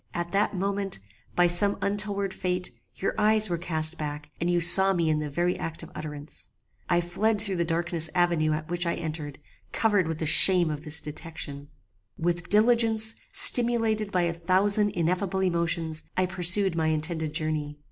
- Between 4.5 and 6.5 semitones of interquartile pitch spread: No, average, 3.8 semitones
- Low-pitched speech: No, medium, 175 Hz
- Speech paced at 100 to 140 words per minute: No, average, 175 wpm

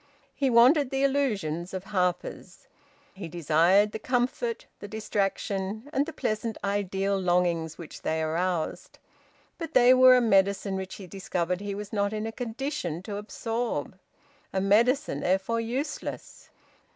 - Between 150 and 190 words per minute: No, average, 140 wpm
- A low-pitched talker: No, high, 205 Hz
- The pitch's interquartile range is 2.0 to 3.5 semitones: No, average, 4.7 semitones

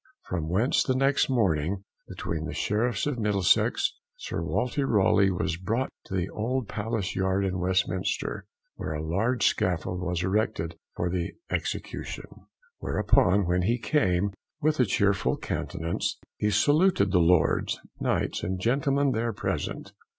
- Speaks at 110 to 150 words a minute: Yes, average, 145 wpm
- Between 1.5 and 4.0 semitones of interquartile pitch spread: No, average, 5.1 semitones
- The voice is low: Yes, low, 100 Hz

